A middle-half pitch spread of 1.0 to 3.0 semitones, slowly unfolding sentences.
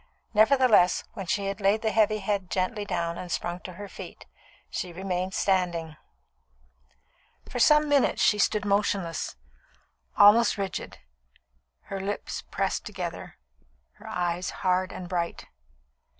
Yes: narrow, 2.6 semitones; slow, 130 wpm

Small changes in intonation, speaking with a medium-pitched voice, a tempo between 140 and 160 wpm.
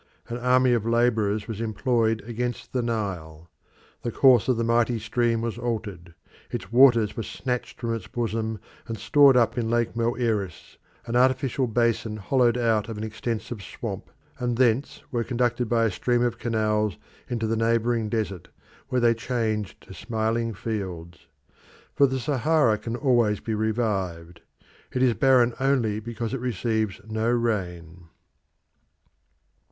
No: narrow, 2.1 semitones; low, 115 Hz; average, 150 wpm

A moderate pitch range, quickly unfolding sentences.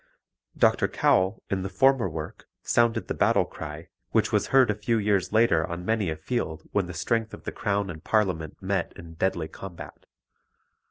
No: average, 4.6 semitones; average, 180 wpm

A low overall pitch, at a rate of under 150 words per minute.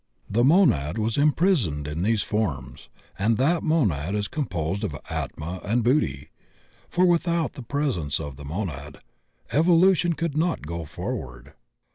Yes: low, 110 Hz; average, 140 wpm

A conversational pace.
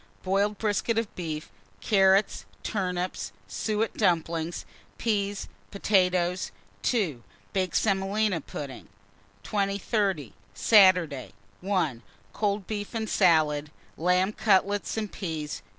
No: slow, 95 wpm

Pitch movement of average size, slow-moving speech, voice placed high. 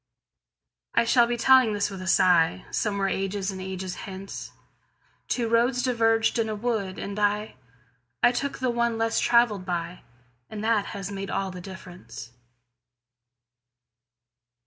Yes: average, 3.9 semitones; slow, 125 wpm; high, 200 Hz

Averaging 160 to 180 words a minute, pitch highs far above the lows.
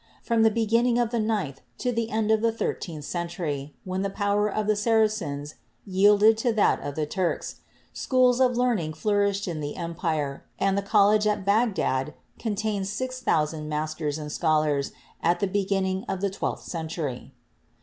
Yes: average, 170 wpm; wide, 5.7 semitones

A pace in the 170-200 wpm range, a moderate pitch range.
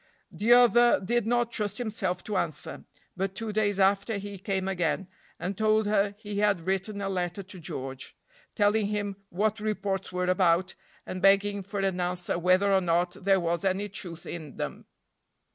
No: average, 175 wpm; narrow, 2.3 semitones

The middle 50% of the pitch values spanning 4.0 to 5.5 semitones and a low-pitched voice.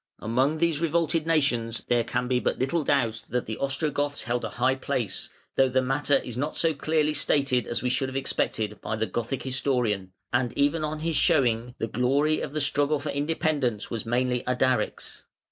No: average, 3.4 semitones; low, 130 Hz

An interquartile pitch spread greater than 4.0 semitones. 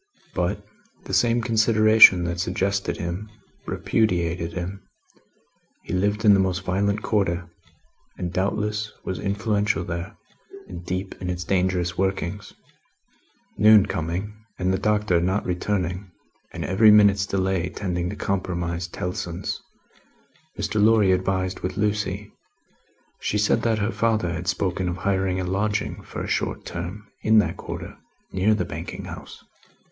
No: narrow, 2.6 semitones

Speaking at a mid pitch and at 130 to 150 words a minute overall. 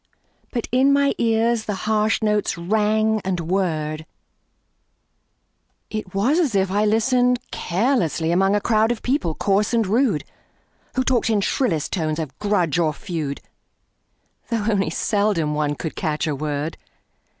No: high, 205 Hz; average, 145 wpm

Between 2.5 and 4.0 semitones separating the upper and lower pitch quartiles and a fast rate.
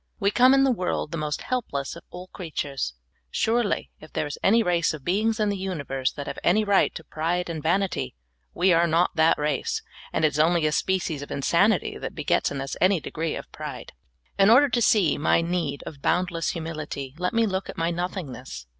No: average, 4.4 semitones; fast, 210 wpm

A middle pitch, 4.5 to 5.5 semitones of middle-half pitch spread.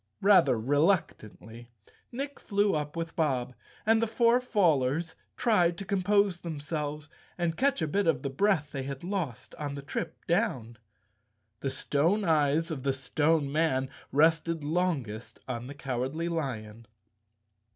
Yes: medium, 155 Hz; average, 5.0 semitones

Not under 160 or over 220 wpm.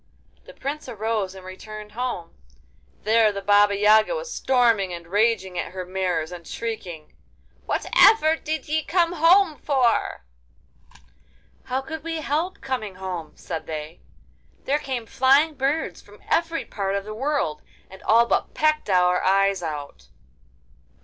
No: average, 145 wpm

